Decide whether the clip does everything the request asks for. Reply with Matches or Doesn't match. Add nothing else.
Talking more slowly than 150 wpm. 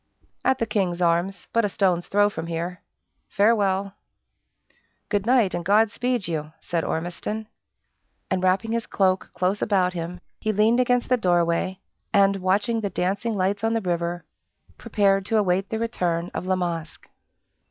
Doesn't match